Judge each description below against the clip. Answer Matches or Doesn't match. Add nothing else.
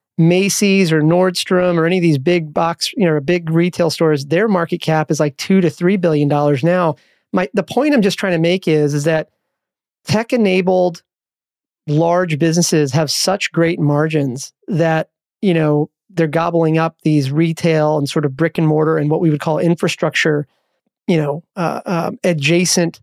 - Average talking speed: Matches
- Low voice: Doesn't match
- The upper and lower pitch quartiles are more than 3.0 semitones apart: Doesn't match